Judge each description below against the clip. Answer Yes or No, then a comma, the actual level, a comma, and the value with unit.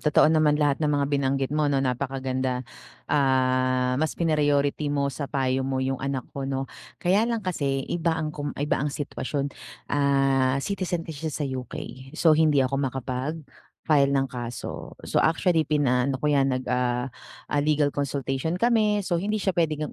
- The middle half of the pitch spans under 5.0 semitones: Yes, average, 2.7 semitones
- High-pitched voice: No, medium, 140 Hz